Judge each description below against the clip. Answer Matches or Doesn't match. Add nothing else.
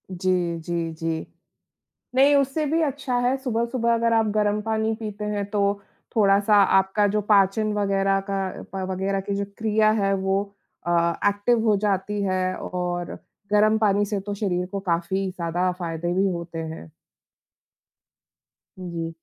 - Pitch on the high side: Matches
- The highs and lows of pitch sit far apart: Doesn't match